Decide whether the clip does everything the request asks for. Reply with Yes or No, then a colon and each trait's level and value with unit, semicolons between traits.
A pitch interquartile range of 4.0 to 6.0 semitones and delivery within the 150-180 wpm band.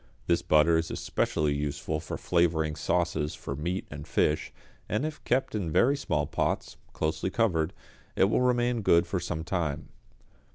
Yes: average, 4.6 semitones; average, 160 wpm